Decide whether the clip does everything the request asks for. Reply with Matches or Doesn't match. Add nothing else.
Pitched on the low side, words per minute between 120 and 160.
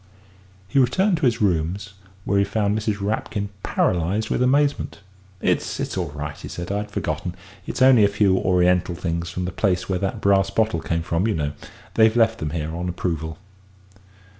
Doesn't match